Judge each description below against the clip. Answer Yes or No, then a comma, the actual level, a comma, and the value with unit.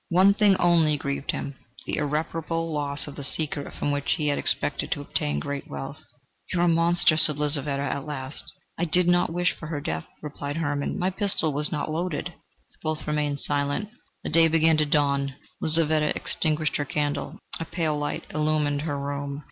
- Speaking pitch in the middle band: Yes, medium, 150 Hz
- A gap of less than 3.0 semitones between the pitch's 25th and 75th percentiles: Yes, narrow, 2.5 semitones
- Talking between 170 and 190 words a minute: Yes, average, 185 wpm